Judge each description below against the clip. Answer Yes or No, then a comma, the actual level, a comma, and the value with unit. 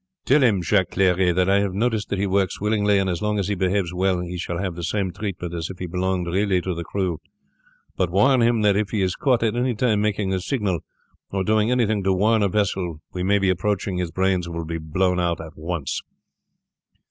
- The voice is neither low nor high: No, very low, 95 Hz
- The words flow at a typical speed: No, fast, 230 wpm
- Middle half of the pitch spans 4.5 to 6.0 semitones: No, average, 2.7 semitones